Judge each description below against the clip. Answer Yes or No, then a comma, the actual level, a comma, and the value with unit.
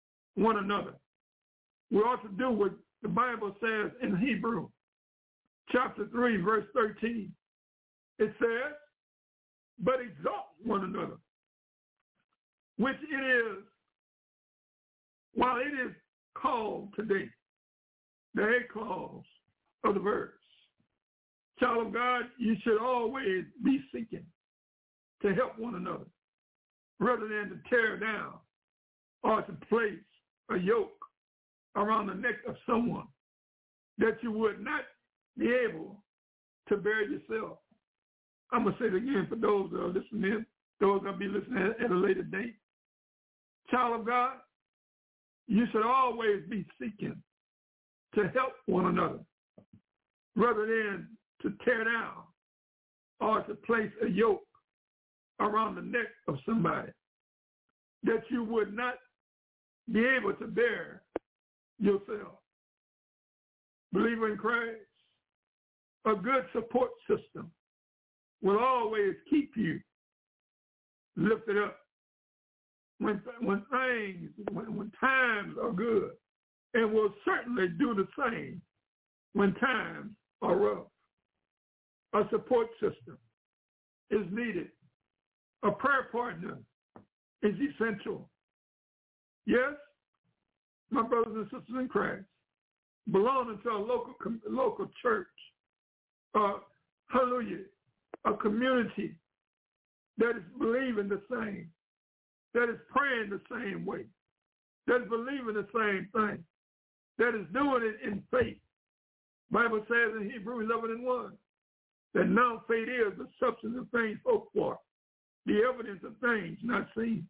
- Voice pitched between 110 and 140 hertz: No, high, 225 Hz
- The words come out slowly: Yes, slow, 120 wpm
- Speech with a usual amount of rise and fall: Yes, average, 3.1 semitones